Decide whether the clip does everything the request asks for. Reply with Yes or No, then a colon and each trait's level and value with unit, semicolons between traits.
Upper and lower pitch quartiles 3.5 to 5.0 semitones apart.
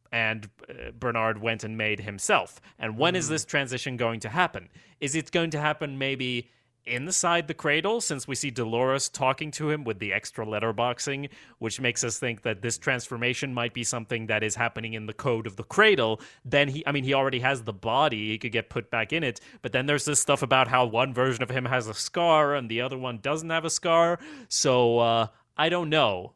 Yes: average, 4.3 semitones